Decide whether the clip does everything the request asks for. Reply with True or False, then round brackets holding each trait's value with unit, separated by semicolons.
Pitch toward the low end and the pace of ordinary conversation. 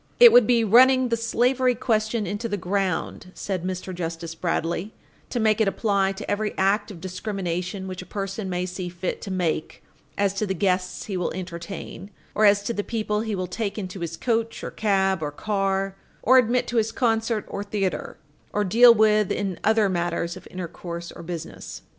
False (195 Hz; 190 wpm)